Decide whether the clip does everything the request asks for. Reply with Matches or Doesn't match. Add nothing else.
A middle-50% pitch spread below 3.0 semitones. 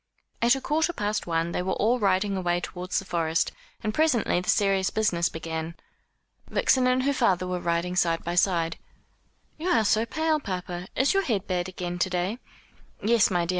Doesn't match